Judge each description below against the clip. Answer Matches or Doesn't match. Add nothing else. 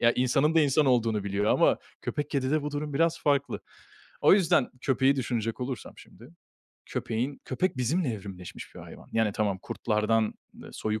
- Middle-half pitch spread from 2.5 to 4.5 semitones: Doesn't match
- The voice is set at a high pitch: Doesn't match